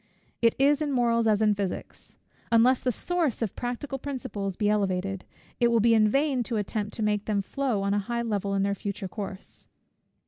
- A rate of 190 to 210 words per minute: Yes, average, 200 wpm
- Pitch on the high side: Yes, high, 220 Hz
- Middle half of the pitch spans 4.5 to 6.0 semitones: No, average, 3.6 semitones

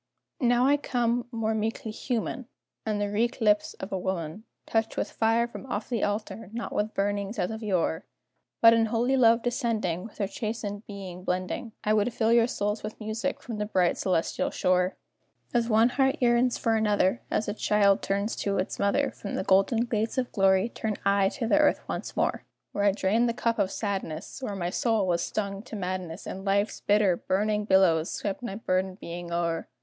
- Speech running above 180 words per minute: Yes, average, 195 wpm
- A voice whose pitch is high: Yes, high, 210 Hz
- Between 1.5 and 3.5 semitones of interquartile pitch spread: Yes, average, 3.1 semitones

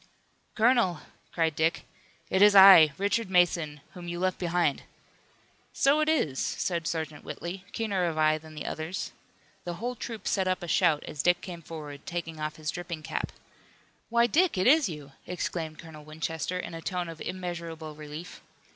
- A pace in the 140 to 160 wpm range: No, average, 175 wpm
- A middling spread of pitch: Yes, average, 3.2 semitones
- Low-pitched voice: No, medium, 170 Hz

